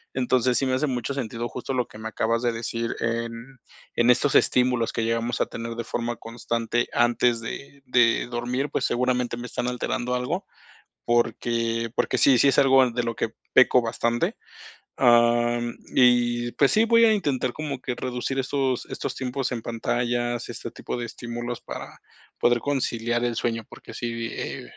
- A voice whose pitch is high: No, low, 120 Hz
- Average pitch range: No, narrow, 1.4 semitones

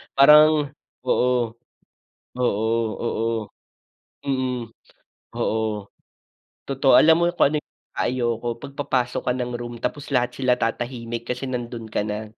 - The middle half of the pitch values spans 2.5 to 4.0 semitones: Yes, average, 2.8 semitones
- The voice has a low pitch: Yes, low, 125 Hz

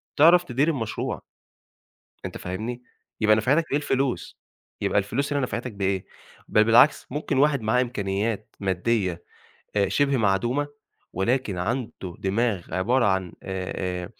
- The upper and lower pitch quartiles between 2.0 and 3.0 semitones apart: No, wide, 5.4 semitones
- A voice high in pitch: No, low, 115 Hz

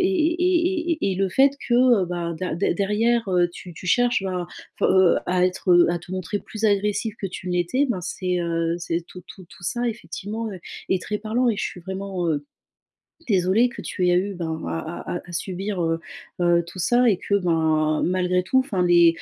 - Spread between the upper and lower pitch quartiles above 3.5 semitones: Yes, average, 4.0 semitones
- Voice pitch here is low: No, medium, 185 Hz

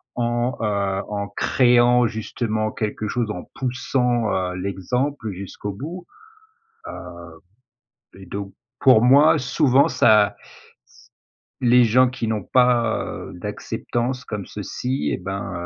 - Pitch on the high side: No, low, 115 Hz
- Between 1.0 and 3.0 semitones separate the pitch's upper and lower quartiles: No, average, 3.7 semitones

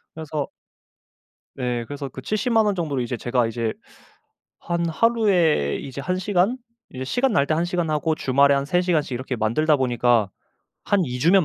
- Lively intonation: Yes, wide, 6.1 semitones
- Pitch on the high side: No, medium, 150 Hz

